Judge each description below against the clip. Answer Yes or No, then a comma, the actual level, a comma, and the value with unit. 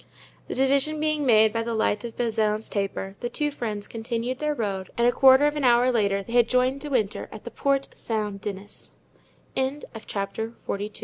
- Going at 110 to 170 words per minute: No, average, 190 wpm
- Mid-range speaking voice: No, high, 235 Hz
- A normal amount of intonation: Yes, average, 3.9 semitones